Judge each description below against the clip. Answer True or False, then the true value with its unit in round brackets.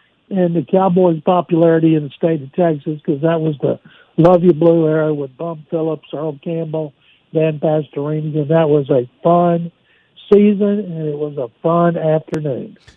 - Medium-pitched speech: True (165 Hz)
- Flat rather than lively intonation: True (1.9 semitones)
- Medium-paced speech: True (165 wpm)